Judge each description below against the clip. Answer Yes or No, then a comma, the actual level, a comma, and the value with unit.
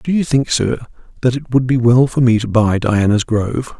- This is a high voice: No, low, 120 Hz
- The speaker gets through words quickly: Yes, fast, 235 wpm